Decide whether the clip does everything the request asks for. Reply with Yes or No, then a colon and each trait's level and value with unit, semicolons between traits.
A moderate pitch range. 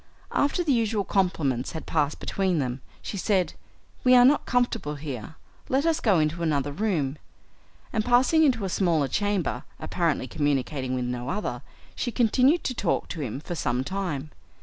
No: wide, 8.0 semitones